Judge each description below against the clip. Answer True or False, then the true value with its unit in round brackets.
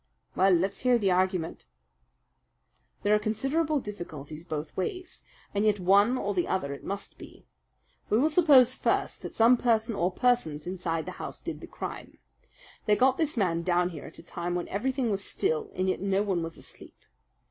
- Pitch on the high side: True (200 Hz)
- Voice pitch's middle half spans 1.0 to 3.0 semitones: False (5.5 semitones)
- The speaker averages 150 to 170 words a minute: False (185 wpm)